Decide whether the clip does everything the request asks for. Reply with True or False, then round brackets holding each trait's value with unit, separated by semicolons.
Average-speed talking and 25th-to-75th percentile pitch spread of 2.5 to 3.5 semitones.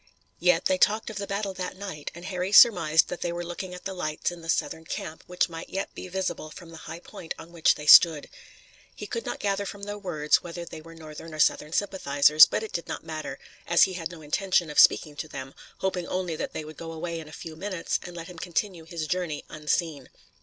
False (240 wpm; 2.8 semitones)